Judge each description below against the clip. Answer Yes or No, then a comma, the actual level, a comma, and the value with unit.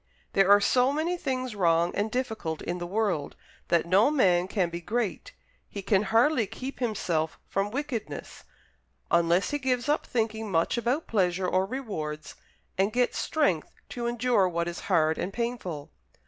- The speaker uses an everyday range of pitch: No, wide, 5.9 semitones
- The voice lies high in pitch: Yes, high, 205 Hz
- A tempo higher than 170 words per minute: No, average, 160 wpm